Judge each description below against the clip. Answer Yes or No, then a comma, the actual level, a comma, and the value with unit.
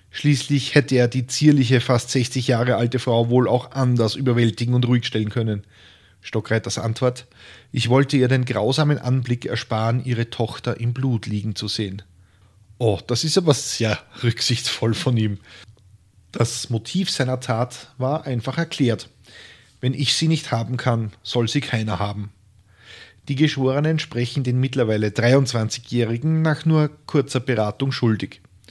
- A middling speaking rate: Yes, average, 145 wpm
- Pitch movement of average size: Yes, average, 3.1 semitones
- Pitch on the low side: Yes, low, 120 Hz